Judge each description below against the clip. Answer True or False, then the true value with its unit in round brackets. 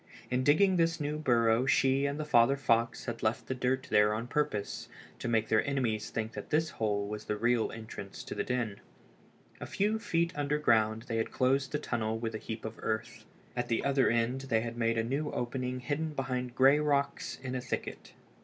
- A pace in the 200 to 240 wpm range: True (205 wpm)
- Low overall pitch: True (125 Hz)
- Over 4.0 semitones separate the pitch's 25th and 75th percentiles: False (3.7 semitones)